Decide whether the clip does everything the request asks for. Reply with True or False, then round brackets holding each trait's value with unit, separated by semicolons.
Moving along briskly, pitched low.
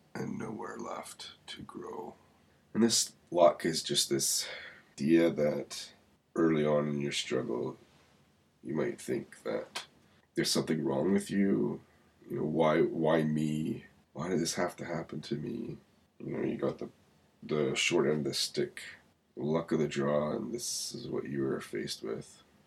False (165 wpm; 75 Hz)